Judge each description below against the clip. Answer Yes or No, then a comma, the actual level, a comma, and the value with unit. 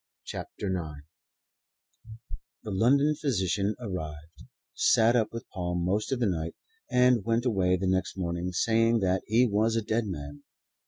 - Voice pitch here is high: No, low, 100 Hz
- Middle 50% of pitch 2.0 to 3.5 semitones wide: No, average, 4.3 semitones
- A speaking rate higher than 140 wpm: Yes, average, 150 wpm